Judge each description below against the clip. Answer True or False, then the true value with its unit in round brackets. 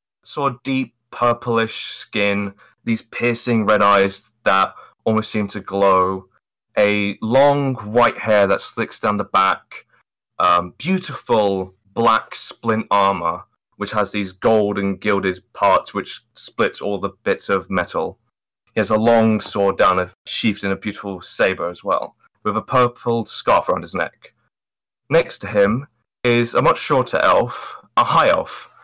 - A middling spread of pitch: True (3.1 semitones)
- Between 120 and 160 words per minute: True (155 wpm)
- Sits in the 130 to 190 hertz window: False (105 Hz)